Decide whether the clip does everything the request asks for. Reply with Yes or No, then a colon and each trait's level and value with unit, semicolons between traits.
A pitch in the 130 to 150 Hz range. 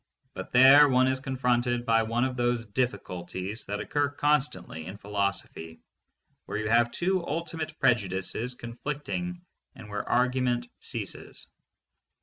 No: low, 120 Hz